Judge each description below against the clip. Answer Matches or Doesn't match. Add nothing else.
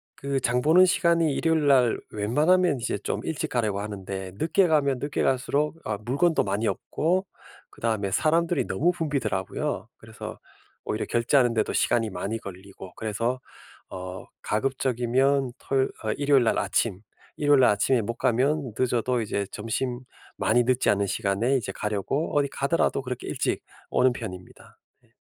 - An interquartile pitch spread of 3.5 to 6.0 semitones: Matches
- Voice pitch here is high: Doesn't match